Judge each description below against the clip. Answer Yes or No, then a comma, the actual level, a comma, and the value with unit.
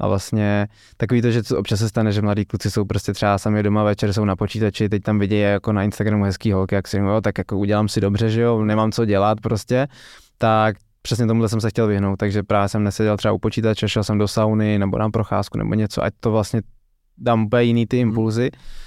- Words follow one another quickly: Yes, fast, 240 wpm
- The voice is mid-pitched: No, low, 105 Hz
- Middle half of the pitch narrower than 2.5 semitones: Yes, narrow, 1.4 semitones